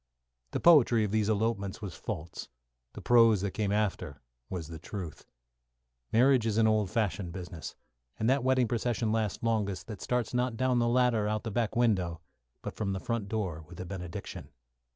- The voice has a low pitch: Yes, low, 110 Hz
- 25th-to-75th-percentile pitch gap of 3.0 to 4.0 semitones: Yes, average, 3.7 semitones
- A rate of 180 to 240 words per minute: Yes, average, 185 wpm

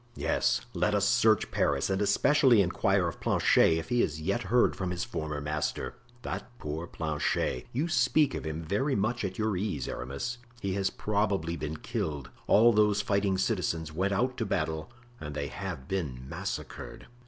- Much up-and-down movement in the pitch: Yes, wide, 5.7 semitones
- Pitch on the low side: Yes, very low, 95 Hz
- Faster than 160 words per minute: Yes, average, 175 wpm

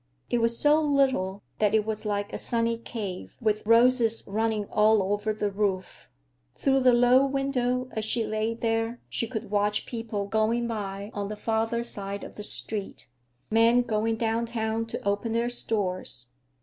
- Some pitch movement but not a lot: No, narrow, 2.1 semitones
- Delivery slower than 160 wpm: No, average, 165 wpm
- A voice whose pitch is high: Yes, high, 225 Hz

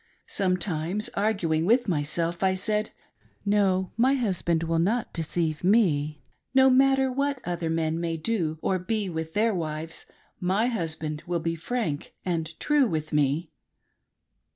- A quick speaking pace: No, average, 140 wpm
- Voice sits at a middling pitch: Yes, medium, 175 Hz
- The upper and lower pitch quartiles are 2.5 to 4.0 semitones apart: No, average, 4.9 semitones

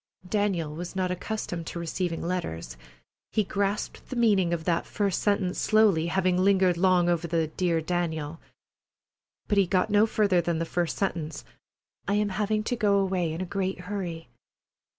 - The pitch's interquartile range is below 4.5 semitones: Yes, average, 3.0 semitones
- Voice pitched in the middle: Yes, medium, 180 Hz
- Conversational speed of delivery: Yes, average, 170 wpm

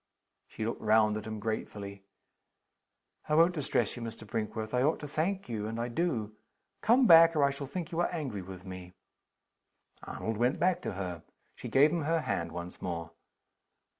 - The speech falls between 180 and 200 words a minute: Yes, average, 185 wpm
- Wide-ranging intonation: Yes, wide, 7.3 semitones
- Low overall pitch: Yes, low, 115 Hz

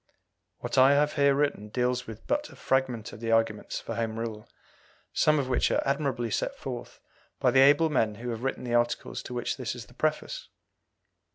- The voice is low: Yes, low, 125 Hz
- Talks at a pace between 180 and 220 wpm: Yes, average, 200 wpm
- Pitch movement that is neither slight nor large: Yes, average, 3.7 semitones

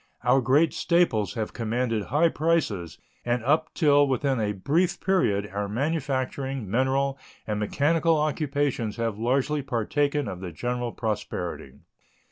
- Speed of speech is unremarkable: No, slow, 130 wpm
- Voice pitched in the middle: No, low, 130 Hz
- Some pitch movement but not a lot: Yes, average, 4.9 semitones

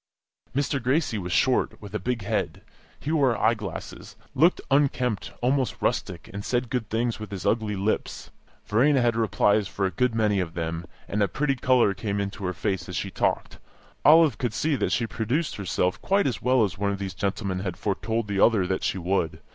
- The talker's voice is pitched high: No, low, 110 Hz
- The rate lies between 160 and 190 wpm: No, fast, 205 wpm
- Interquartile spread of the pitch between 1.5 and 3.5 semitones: No, average, 4.3 semitones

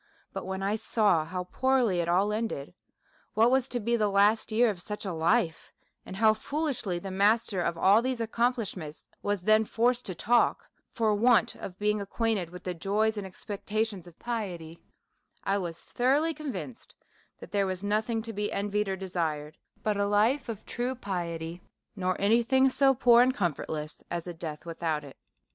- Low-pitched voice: No, high, 205 Hz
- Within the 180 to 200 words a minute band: Yes, average, 185 wpm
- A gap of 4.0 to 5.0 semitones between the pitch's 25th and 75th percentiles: Yes, average, 4.4 semitones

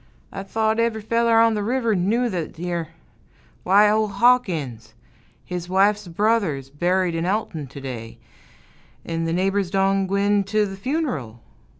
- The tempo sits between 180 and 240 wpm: No, average, 150 wpm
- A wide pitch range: No, average, 4.7 semitones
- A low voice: No, high, 195 Hz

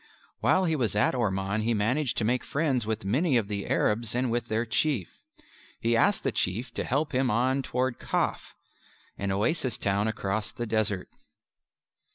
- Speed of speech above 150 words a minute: Yes, average, 175 wpm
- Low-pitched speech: Yes, low, 115 Hz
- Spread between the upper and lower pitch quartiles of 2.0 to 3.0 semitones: No, average, 3.7 semitones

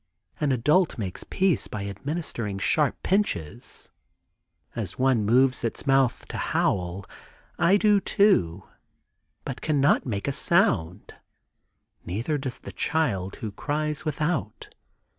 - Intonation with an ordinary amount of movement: No, wide, 7.6 semitones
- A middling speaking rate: No, slow, 120 wpm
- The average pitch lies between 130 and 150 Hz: Yes, low, 135 Hz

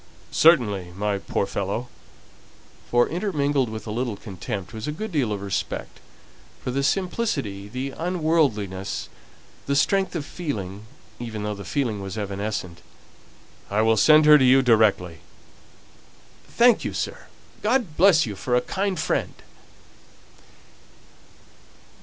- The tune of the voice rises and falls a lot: Yes, wide, 7.4 semitones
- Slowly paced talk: Yes, slow, 130 wpm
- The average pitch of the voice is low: Yes, low, 120 Hz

